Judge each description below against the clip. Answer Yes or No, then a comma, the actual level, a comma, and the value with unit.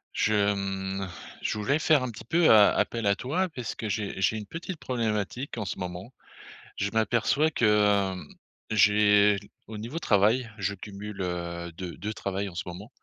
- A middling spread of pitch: Yes, average, 3.1 semitones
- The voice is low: Yes, low, 105 Hz